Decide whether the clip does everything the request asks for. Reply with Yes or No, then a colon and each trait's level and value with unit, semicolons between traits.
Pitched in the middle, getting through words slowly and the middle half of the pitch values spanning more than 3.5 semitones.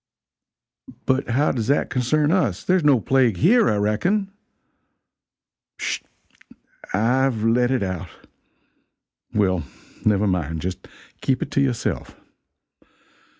No: low, 120 Hz; slow, 115 wpm; average, 5.2 semitones